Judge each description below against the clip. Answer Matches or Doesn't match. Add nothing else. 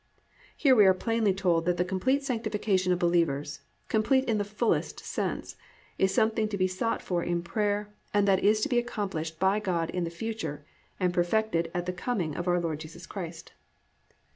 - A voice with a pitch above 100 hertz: Matches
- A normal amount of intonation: Matches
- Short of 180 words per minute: Doesn't match